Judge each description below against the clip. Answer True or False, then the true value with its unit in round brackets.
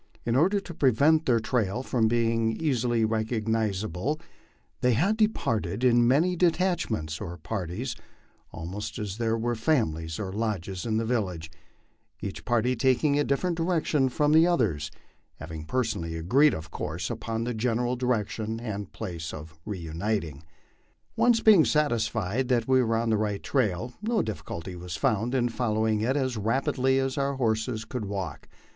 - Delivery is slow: False (160 wpm)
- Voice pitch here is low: True (115 Hz)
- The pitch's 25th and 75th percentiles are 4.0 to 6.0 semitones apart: True (4.5 semitones)